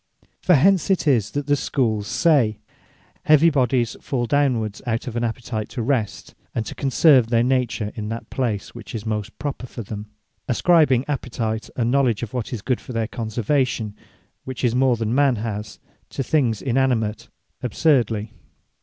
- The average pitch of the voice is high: No, low, 120 Hz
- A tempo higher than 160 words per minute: Yes, average, 170 wpm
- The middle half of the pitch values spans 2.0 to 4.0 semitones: Yes, average, 3.4 semitones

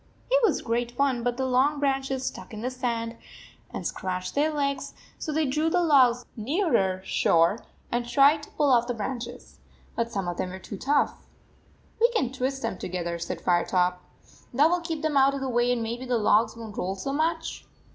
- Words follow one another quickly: Yes, fast, 215 wpm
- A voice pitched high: Yes, very high, 250 Hz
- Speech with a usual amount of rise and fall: Yes, average, 3.9 semitones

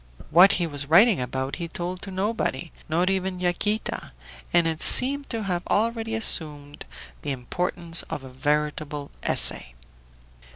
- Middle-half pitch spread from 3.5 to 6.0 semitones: Yes, average, 4.9 semitones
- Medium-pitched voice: Yes, medium, 175 Hz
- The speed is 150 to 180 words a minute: No, average, 140 wpm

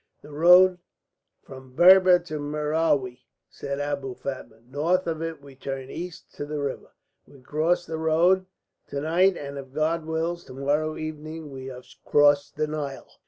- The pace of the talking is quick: No, average, 165 wpm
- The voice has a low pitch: No, medium, 150 Hz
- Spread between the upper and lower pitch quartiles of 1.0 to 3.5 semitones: Yes, average, 3.0 semitones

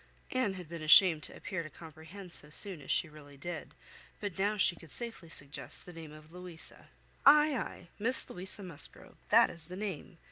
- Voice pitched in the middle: Yes, medium, 175 Hz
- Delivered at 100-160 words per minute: No, average, 190 wpm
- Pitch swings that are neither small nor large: Yes, average, 4.1 semitones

